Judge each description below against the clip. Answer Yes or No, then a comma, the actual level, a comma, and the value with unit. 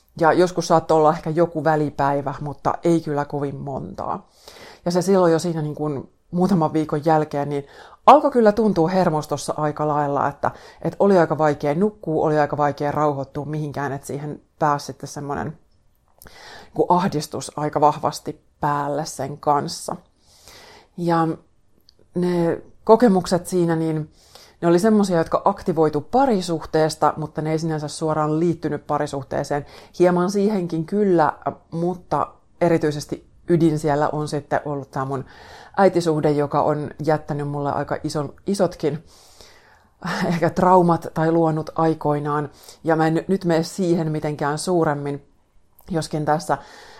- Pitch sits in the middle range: Yes, medium, 155 Hz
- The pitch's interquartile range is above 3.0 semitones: No, average, 2.7 semitones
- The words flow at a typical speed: Yes, average, 135 wpm